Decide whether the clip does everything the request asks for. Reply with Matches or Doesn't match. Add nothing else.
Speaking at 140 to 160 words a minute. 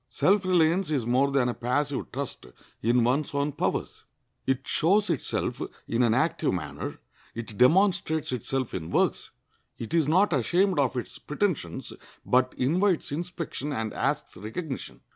Matches